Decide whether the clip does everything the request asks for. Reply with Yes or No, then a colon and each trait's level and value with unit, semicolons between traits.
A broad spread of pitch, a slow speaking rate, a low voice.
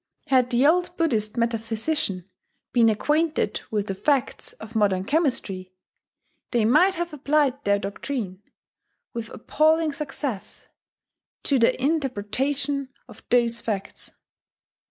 No: wide, 5.7 semitones; slow, 115 wpm; very high, 250 Hz